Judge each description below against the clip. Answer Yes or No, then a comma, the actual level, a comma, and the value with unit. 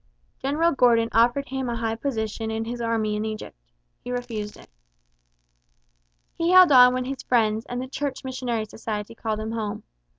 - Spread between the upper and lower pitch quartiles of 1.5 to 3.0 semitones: Yes, average, 2.7 semitones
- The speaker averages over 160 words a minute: Yes, average, 170 wpm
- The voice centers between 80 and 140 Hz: No, high, 235 Hz